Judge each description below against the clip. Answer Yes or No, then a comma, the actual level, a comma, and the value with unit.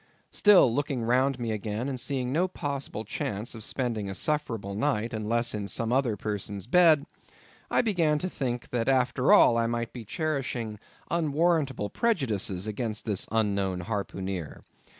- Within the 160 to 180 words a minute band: No, average, 150 wpm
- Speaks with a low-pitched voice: Yes, low, 120 Hz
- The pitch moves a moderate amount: Yes, average, 4.9 semitones